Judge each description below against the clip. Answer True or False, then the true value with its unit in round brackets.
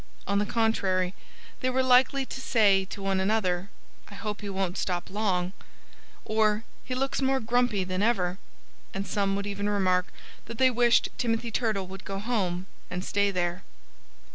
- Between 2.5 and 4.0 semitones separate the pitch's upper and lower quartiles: True (3.5 semitones)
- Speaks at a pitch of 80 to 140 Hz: False (205 Hz)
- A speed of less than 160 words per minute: False (170 wpm)